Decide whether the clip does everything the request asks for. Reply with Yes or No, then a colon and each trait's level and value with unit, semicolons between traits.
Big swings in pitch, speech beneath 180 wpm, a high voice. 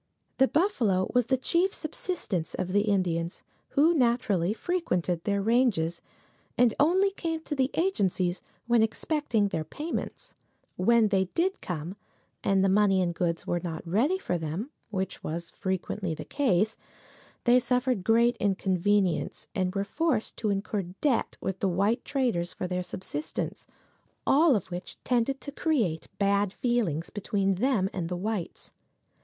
Yes: wide, 5.7 semitones; average, 150 wpm; high, 205 Hz